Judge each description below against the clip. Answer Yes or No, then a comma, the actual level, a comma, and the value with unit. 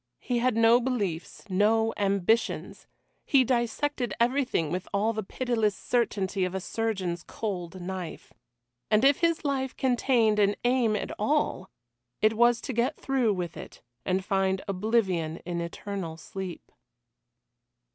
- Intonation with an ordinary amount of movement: Yes, average, 4.3 semitones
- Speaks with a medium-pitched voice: No, high, 215 Hz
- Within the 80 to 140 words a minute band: Yes, slow, 135 wpm